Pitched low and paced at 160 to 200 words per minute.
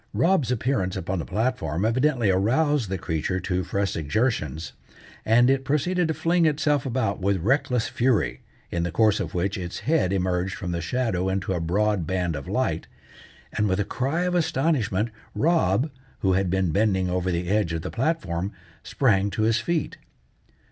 Yes: low, 105 Hz; average, 175 wpm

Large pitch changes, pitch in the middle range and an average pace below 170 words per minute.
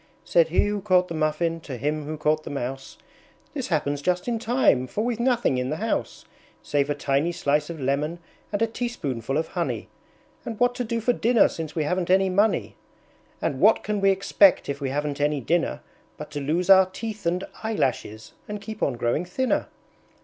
No: wide, 6.2 semitones; medium, 170 Hz; average, 200 wpm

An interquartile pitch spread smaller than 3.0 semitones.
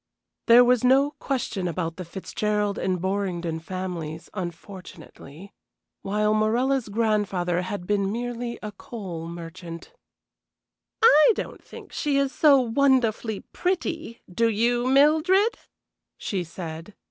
No: wide, 5.6 semitones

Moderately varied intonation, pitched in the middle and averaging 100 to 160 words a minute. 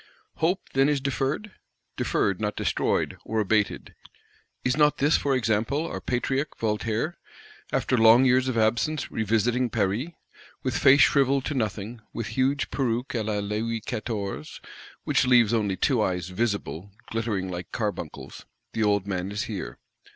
No: average, 4.2 semitones; low, 115 Hz; average, 150 wpm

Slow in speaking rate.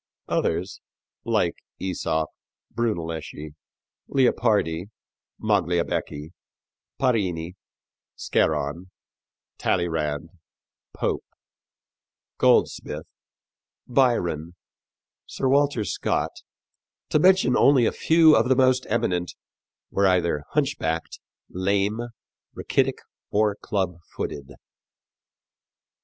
Yes: slow, 70 wpm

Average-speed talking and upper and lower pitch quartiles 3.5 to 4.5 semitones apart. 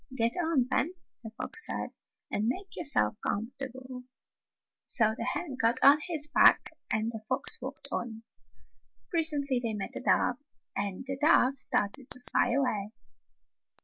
Yes: average, 145 wpm; average, 3.9 semitones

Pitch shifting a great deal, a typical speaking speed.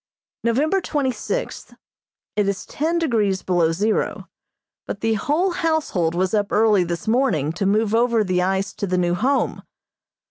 Yes: wide, 6.2 semitones; average, 155 wpm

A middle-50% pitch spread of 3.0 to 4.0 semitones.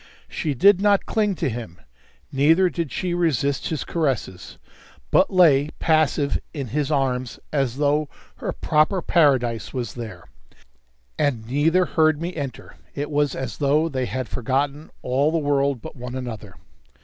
Yes: average, 3.7 semitones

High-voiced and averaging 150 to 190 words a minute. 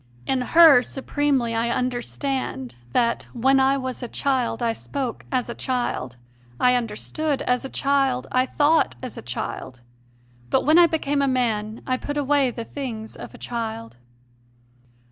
Yes: very high, 255 Hz; average, 165 wpm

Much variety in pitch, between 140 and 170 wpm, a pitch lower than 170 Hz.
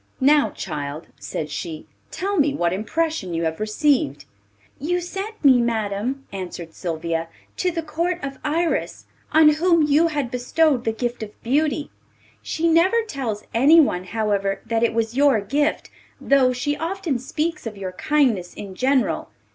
No: wide, 7.4 semitones; average, 155 wpm; very high, 265 Hz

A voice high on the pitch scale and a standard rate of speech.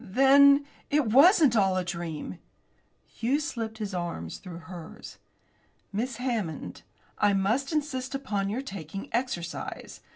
No: high, 220 Hz; slow, 125 wpm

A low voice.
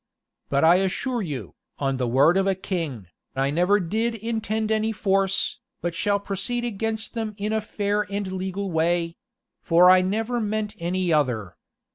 No: high, 195 Hz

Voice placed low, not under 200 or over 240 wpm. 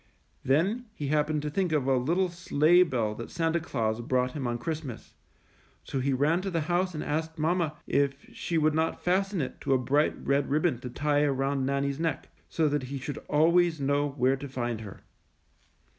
No: medium, 145 Hz; fast, 205 wpm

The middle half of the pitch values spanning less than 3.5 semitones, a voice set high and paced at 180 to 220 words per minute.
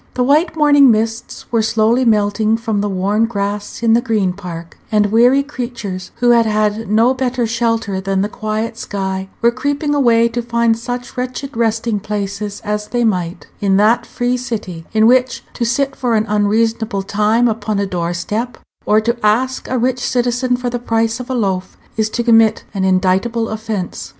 Yes: average, 2.8 semitones; high, 225 Hz; average, 185 wpm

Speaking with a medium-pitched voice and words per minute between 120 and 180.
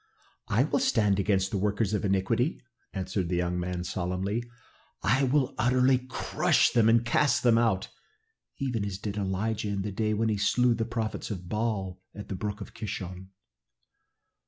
No: low, 105 Hz; average, 170 wpm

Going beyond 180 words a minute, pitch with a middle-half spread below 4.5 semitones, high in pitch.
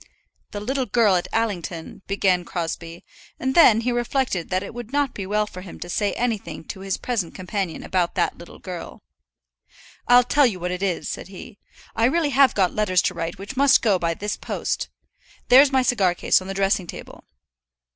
No: average, 200 wpm; average, 5.1 semitones; high, 200 Hz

